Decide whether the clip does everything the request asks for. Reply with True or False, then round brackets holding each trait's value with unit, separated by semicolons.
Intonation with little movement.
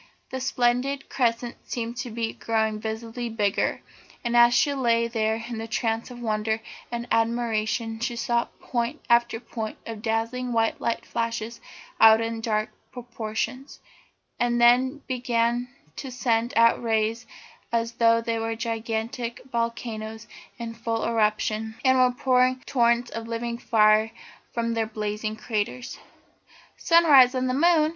True (1.4 semitones)